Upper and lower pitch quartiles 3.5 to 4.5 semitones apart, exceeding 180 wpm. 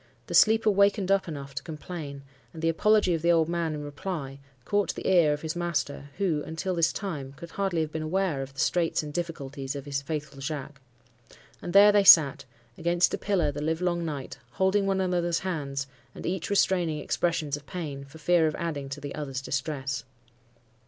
Yes: average, 4.0 semitones; average, 195 wpm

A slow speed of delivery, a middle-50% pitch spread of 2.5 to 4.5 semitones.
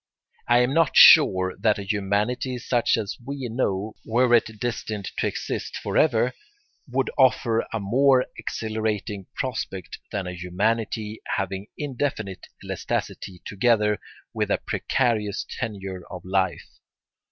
Yes: slow, 130 wpm; average, 3.9 semitones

